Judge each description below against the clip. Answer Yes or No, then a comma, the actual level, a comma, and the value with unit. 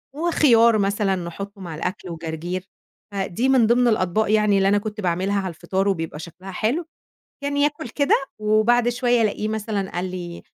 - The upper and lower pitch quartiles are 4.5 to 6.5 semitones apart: No, average, 4.1 semitones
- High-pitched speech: Yes, high, 205 Hz